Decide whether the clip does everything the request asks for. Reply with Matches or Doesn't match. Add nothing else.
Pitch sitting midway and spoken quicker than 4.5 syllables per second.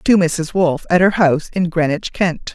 Matches